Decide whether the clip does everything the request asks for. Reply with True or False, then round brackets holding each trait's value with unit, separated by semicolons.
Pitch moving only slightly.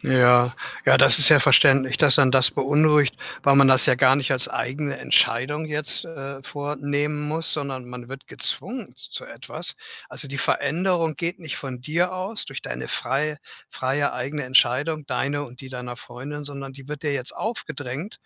True (2.3 semitones)